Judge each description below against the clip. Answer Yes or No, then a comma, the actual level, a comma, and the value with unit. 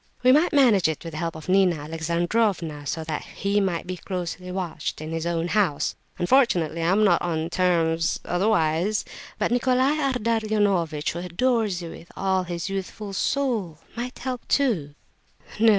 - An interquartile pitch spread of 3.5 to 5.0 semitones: Yes, average, 4.7 semitones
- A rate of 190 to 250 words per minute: No, average, 165 wpm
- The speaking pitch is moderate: Yes, medium, 180 Hz